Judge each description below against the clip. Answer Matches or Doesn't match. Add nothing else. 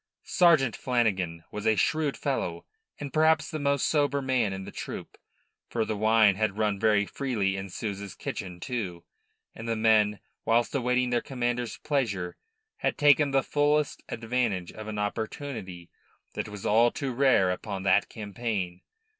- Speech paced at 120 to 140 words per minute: Doesn't match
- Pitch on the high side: Doesn't match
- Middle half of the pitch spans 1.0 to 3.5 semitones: Doesn't match